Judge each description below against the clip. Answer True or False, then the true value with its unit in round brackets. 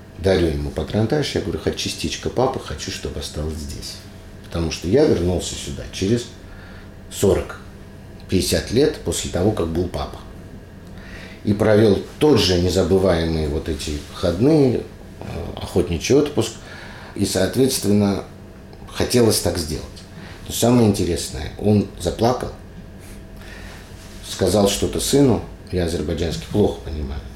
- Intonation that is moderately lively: True (3.0 semitones)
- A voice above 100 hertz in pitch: False (95 Hz)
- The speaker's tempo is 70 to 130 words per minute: True (115 wpm)